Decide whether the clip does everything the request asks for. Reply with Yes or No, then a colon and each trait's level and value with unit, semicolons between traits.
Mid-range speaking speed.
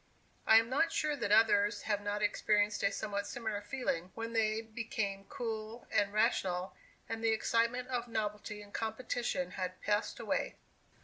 Yes: average, 160 wpm